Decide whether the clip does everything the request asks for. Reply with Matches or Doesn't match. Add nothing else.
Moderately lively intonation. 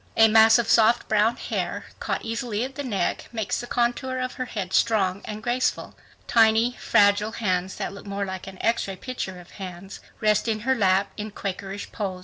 Matches